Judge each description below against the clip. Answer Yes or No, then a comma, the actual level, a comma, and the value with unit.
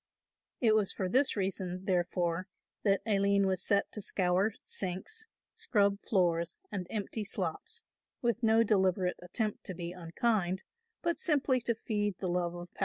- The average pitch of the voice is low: No, high, 195 Hz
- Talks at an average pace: Yes, average, 155 wpm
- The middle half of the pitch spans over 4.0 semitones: No, average, 3.4 semitones